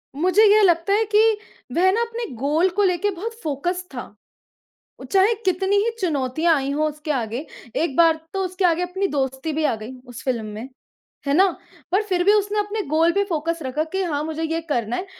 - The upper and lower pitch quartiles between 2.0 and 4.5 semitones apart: No, average, 5.1 semitones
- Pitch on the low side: No, very high, 335 Hz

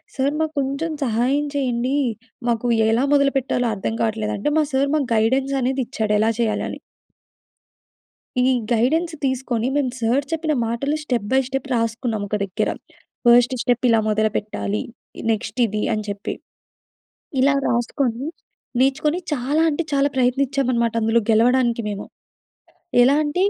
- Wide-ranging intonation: No, average, 3.5 semitones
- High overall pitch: Yes, very high, 250 Hz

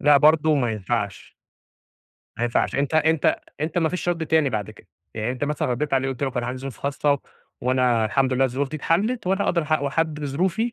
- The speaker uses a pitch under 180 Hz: Yes, medium, 140 Hz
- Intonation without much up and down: No, average, 3.9 semitones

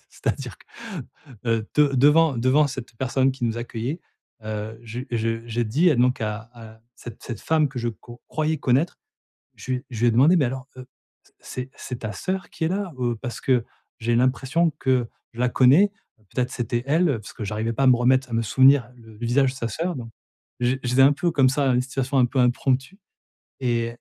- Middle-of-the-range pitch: No, low, 125 Hz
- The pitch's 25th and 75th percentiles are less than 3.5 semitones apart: Yes, average, 2.8 semitones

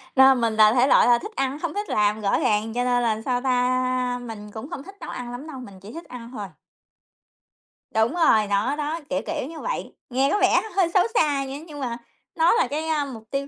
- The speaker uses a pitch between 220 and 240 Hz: No, very high, 255 Hz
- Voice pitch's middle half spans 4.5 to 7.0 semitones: Yes, average, 4.8 semitones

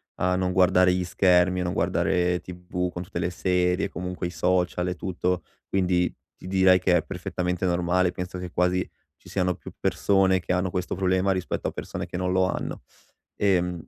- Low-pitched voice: Yes, very low, 90 Hz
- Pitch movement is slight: Yes, narrow, 0.7 semitones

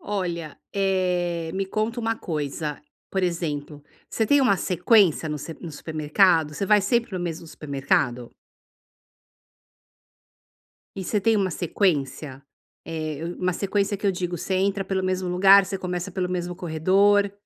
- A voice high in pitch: No, medium, 180 Hz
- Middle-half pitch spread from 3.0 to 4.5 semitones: Yes, average, 3.5 semitones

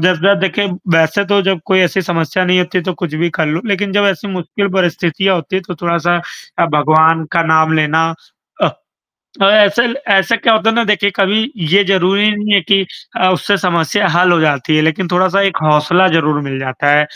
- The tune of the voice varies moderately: Yes, average, 3.6 semitones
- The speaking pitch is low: No, medium, 180 Hz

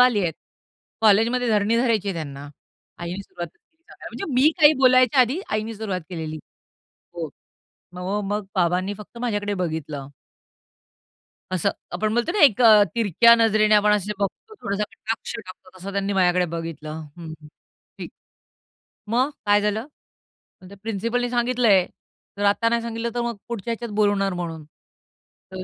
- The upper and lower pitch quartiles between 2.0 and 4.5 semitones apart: Yes, average, 4.1 semitones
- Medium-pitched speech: No, high, 205 Hz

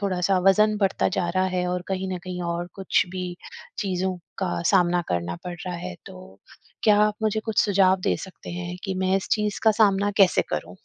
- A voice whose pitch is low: No, medium, 185 Hz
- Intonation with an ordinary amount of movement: No, narrow, 1.7 semitones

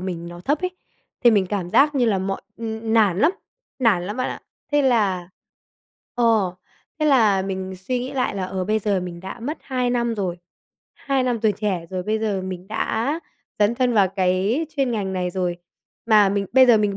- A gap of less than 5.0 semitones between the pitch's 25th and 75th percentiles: Yes, average, 4.4 semitones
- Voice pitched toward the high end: Yes, high, 210 Hz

